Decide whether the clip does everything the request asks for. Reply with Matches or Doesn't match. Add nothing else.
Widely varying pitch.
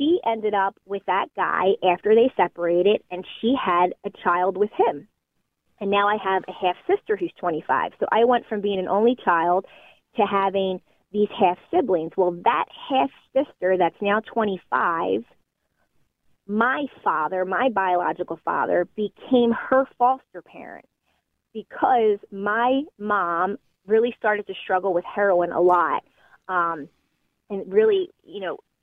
Doesn't match